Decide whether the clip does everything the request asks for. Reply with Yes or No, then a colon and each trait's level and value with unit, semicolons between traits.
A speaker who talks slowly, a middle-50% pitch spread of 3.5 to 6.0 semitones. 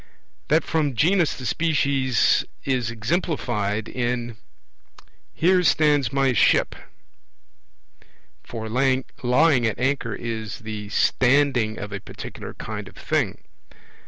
Yes: slow, 105 wpm; average, 4.5 semitones